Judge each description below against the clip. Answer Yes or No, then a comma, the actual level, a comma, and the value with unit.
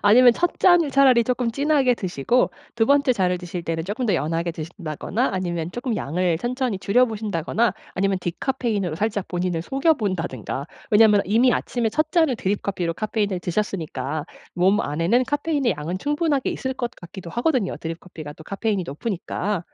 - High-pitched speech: Yes, high, 205 Hz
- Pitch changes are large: Yes, wide, 6.3 semitones